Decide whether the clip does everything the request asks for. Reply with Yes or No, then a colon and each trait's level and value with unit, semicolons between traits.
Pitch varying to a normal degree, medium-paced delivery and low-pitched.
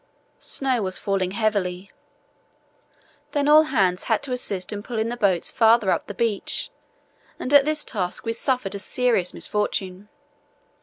No: average, 4.7 semitones; average, 150 wpm; high, 210 Hz